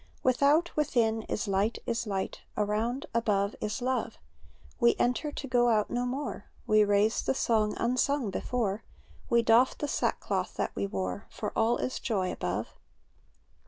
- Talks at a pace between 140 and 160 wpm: Yes, average, 155 wpm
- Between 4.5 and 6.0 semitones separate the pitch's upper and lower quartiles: No, average, 3.1 semitones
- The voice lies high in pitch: Yes, high, 230 Hz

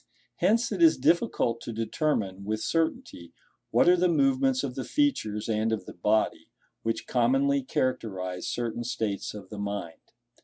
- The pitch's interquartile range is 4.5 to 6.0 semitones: Yes, average, 5.1 semitones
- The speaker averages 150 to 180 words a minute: Yes, average, 155 wpm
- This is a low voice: Yes, low, 115 Hz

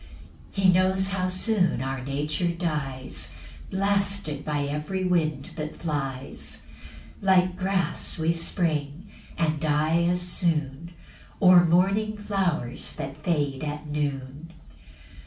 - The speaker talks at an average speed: No, slow, 115 wpm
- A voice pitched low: No, medium, 165 Hz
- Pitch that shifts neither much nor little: Yes, average, 4.0 semitones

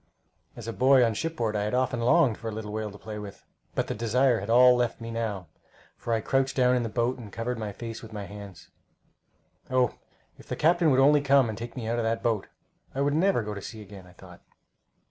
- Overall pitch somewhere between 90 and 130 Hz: Yes, low, 115 Hz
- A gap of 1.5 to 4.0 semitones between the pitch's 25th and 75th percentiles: Yes, average, 3.3 semitones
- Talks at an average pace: No, fast, 240 wpm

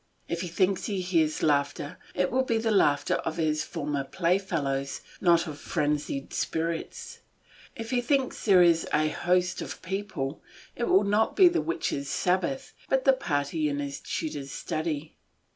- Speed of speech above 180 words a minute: No, average, 160 wpm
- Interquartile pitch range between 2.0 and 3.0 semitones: No, average, 4.8 semitones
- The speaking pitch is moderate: Yes, medium, 170 Hz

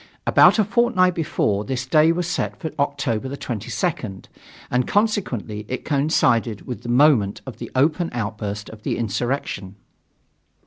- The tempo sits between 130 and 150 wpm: Yes, average, 140 wpm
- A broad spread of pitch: Yes, wide, 6.4 semitones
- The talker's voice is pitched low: Yes, low, 130 Hz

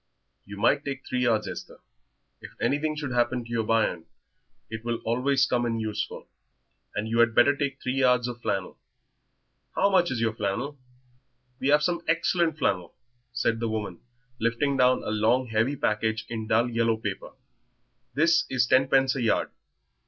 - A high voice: No, low, 120 Hz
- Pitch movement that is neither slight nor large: Yes, average, 3.6 semitones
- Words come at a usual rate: Yes, average, 170 wpm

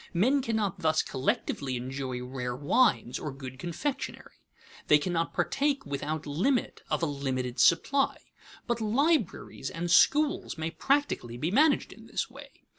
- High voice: No, medium, 165 Hz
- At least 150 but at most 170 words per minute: No, average, 140 wpm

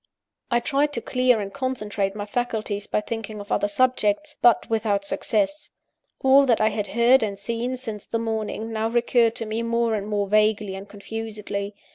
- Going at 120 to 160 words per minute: No, average, 180 wpm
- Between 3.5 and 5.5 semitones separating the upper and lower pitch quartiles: No, narrow, 2.5 semitones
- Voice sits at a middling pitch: No, high, 220 Hz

